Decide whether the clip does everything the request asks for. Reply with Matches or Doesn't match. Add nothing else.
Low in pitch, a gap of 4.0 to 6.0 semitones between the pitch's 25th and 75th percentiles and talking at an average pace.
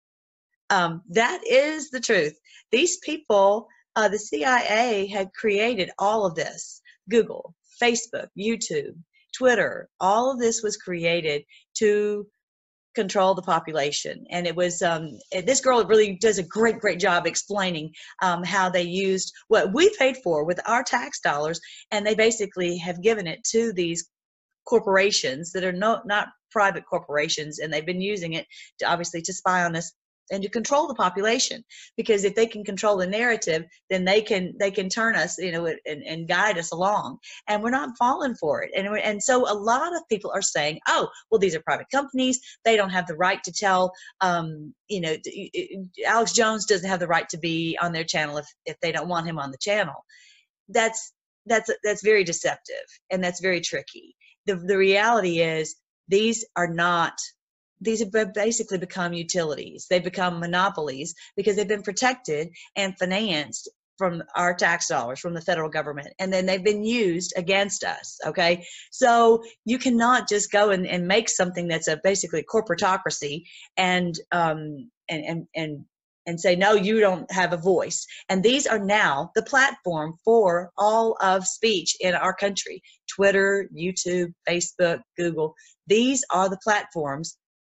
Doesn't match